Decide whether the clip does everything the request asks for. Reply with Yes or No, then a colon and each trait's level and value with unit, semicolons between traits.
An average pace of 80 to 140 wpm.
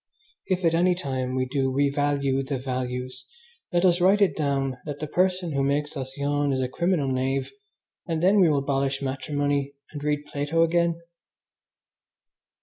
No: average, 165 wpm